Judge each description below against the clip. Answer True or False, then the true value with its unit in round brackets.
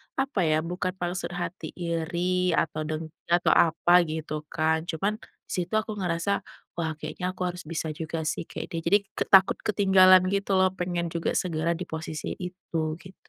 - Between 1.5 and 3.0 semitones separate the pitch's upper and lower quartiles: True (2.6 semitones)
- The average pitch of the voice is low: False (175 Hz)